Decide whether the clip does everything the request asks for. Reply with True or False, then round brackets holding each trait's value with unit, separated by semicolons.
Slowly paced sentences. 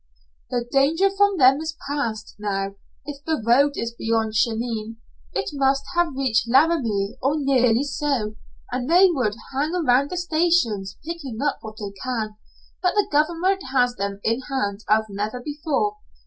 False (160 wpm)